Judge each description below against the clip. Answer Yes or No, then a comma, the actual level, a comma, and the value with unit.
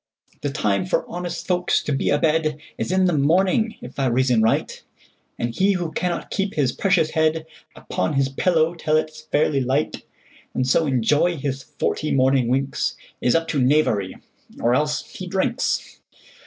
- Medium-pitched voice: Yes, medium, 150 Hz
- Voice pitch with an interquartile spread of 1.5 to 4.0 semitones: No, average, 4.5 semitones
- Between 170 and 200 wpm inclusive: No, average, 155 wpm